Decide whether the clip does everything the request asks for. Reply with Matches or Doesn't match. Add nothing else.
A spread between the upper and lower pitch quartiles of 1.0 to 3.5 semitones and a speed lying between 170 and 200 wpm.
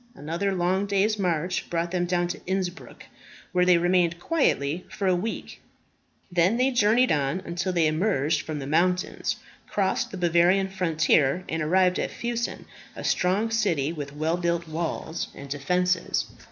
Doesn't match